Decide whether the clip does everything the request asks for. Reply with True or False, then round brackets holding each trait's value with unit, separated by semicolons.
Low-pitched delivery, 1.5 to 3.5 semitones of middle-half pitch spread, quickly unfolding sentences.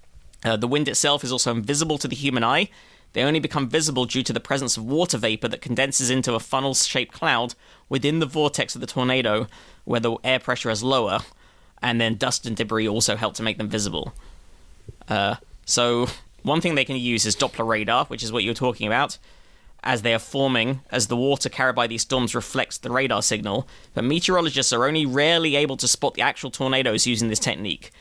True (125 Hz; 3.0 semitones; 210 wpm)